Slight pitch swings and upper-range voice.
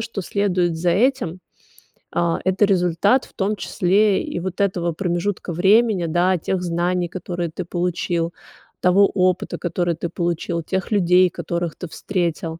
No: narrow, 2.0 semitones; medium, 180 Hz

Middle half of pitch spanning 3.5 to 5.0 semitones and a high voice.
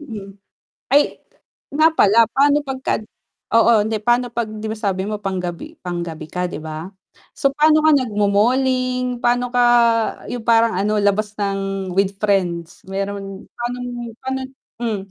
Yes: average, 4.1 semitones; high, 215 Hz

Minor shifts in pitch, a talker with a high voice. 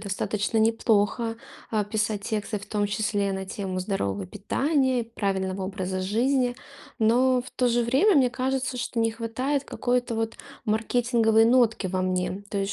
No: average, 3.6 semitones; high, 225 Hz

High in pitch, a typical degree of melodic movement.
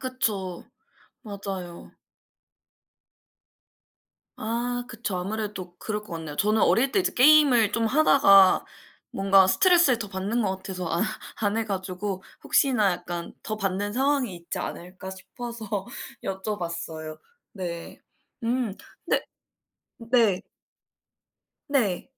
Yes: high, 205 Hz; average, 4.1 semitones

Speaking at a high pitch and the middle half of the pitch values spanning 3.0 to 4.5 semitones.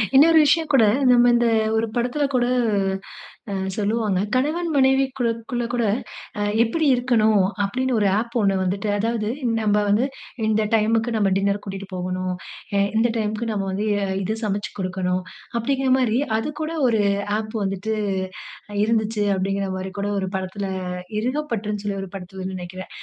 Yes: high, 215 Hz; average, 3.6 semitones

